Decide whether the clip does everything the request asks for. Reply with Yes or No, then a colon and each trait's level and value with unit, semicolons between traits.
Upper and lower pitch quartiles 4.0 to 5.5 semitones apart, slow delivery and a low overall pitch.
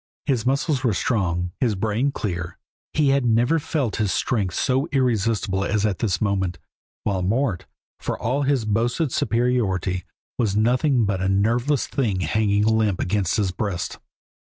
No: average, 4.6 semitones; average, 155 wpm; low, 110 Hz